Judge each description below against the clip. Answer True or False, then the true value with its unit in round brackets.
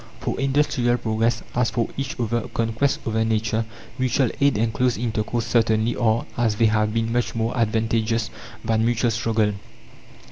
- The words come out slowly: False (155 wpm)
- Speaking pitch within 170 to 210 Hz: False (115 Hz)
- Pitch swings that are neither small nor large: False (1.5 semitones)